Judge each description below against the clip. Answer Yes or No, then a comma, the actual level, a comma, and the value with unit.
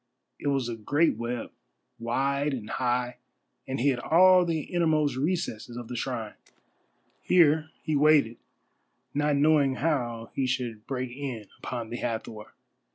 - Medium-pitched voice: No, low, 130 Hz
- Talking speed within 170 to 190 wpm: No, average, 140 wpm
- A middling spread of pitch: Yes, average, 4.0 semitones